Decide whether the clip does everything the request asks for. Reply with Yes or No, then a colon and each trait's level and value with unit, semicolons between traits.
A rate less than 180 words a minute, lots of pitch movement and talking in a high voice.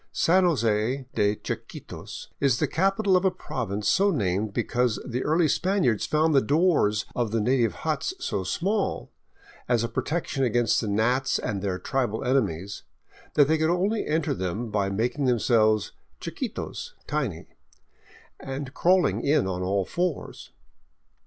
No: average, 145 wpm; wide, 7.0 semitones; low, 125 Hz